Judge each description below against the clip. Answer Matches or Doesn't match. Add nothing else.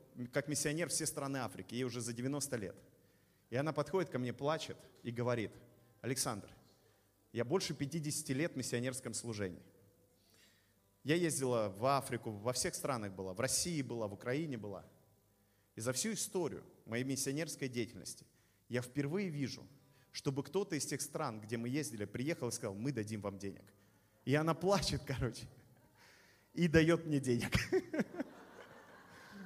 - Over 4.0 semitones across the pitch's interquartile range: Matches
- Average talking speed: Matches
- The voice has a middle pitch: Doesn't match